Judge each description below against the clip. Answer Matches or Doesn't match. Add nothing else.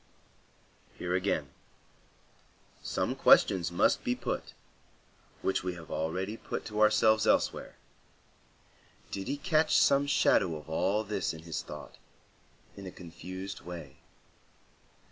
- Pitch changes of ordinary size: Matches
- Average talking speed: Doesn't match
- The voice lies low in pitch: Matches